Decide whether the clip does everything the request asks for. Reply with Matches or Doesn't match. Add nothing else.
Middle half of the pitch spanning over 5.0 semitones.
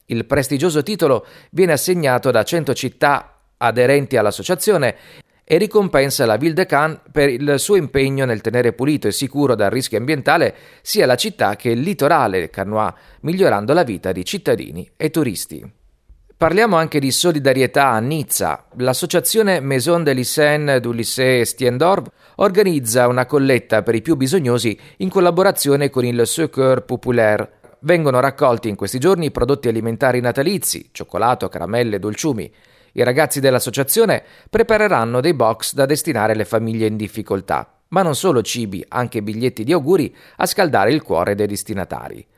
Matches